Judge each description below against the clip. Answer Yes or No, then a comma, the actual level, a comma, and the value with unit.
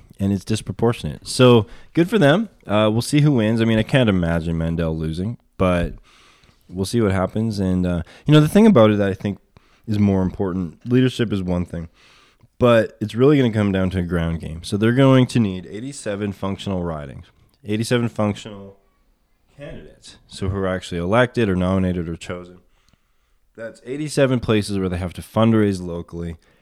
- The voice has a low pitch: Yes, low, 100 Hz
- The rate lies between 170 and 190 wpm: Yes, average, 185 wpm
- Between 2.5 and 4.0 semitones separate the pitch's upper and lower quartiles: No, average, 4.5 semitones